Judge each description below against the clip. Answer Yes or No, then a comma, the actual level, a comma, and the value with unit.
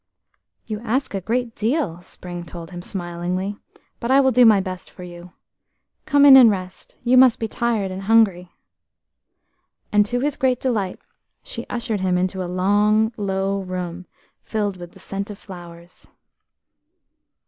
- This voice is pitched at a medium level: No, high, 200 Hz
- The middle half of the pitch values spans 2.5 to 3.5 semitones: No, average, 4.3 semitones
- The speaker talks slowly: No, average, 155 wpm